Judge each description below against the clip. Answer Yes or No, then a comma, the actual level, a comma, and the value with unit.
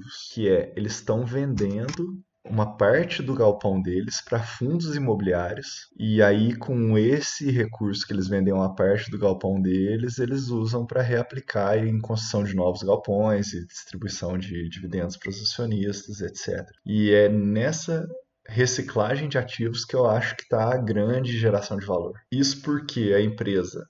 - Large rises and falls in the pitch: No, average, 3.8 semitones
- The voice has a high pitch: No, low, 110 Hz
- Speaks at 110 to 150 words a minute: No, average, 160 wpm